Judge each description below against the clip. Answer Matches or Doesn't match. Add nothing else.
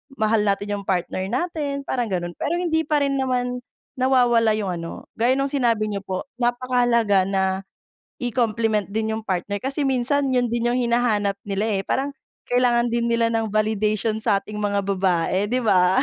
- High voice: Matches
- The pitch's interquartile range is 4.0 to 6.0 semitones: Doesn't match